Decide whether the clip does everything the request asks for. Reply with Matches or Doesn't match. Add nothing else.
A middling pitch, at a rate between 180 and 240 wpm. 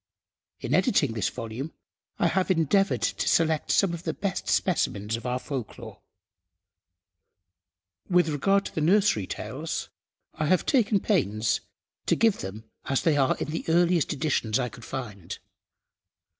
Doesn't match